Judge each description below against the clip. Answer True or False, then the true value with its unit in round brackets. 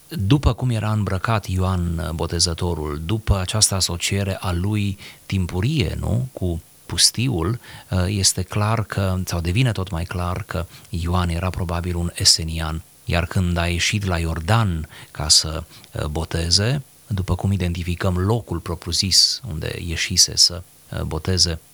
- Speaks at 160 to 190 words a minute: False (130 wpm)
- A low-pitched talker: True (95 Hz)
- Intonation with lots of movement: False (3.5 semitones)